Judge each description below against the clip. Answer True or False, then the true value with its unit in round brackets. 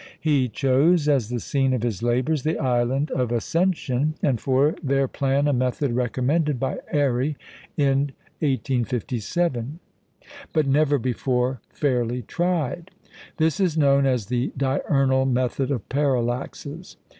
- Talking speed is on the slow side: True (130 wpm)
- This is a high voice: False (135 Hz)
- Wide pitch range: False (2.9 semitones)